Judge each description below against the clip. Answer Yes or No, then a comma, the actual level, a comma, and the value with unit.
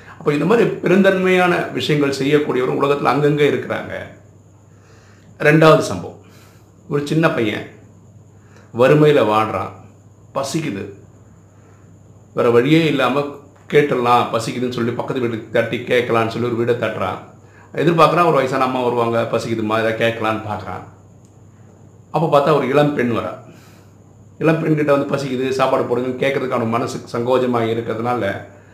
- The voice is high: No, low, 115 Hz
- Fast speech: No, average, 115 wpm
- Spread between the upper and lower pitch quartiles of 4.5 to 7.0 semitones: Yes, average, 4.9 semitones